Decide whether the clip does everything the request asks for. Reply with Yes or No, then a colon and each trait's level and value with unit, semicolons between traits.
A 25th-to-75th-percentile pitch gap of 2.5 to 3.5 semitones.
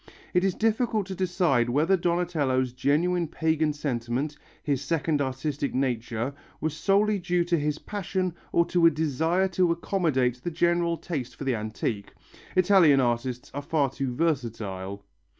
No: average, 5.3 semitones